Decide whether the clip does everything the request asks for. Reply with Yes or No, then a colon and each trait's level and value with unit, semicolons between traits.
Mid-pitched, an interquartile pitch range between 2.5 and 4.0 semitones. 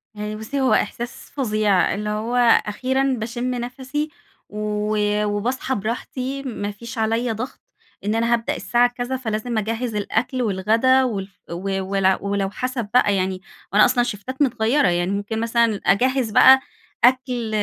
No: high, 225 Hz; average, 3.4 semitones